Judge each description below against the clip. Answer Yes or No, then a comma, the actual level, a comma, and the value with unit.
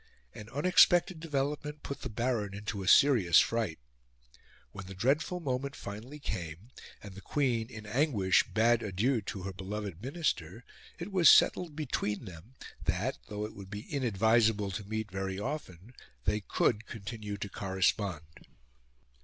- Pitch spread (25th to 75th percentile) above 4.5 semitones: Yes, wide, 5.4 semitones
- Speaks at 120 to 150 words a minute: Yes, average, 145 wpm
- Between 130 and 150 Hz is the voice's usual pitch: No, low, 110 Hz